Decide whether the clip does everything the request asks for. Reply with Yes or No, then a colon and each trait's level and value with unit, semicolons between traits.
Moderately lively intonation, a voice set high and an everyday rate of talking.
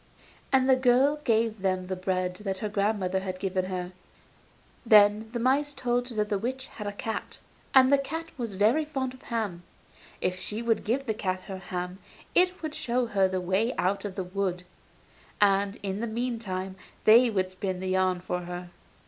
Yes: average, 4.6 semitones; high, 205 Hz; average, 190 wpm